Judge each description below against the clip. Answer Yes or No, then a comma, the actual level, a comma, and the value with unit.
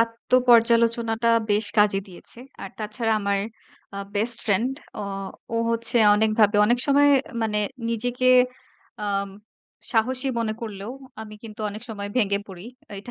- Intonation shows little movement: Yes, narrow, 2.2 semitones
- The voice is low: No, high, 220 Hz